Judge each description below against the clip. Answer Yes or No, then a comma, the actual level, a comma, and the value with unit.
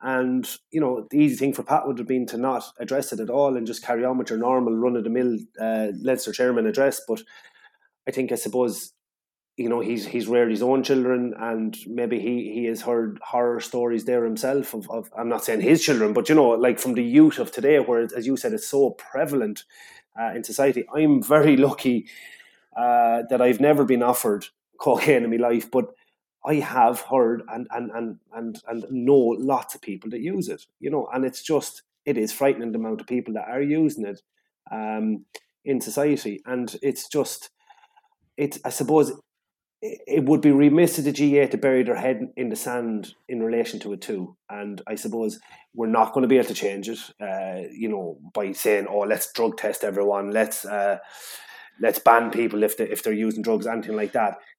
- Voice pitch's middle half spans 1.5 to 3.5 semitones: Yes, average, 3.2 semitones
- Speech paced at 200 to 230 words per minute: Yes, fast, 205 wpm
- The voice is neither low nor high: No, low, 125 Hz